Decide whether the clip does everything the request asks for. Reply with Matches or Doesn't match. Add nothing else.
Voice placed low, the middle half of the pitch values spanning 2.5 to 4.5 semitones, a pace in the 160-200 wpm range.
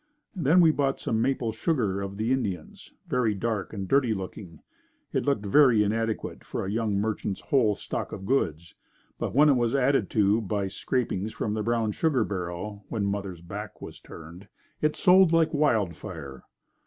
Doesn't match